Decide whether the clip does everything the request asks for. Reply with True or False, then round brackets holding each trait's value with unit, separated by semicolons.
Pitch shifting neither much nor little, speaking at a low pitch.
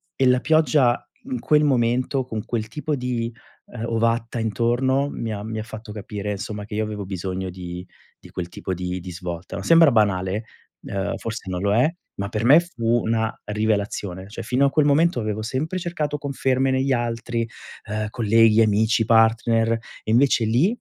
True (3.7 semitones; 115 Hz)